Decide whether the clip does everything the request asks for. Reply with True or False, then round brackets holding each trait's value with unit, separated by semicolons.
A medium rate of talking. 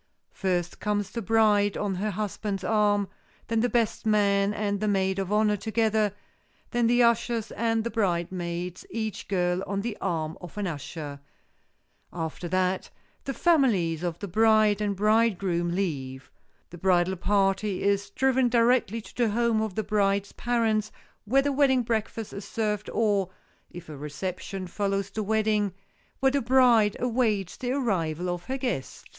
True (160 wpm)